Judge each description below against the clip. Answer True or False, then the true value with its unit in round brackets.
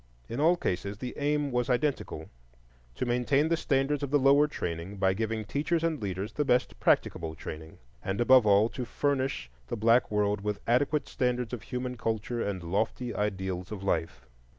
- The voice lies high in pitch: False (115 Hz)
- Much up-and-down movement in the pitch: True (5.8 semitones)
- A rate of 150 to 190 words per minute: True (175 wpm)